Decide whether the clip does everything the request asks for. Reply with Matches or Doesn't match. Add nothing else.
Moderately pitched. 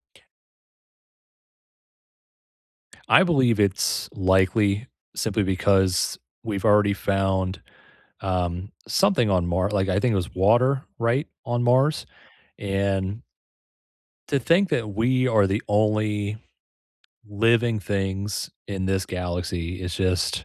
Doesn't match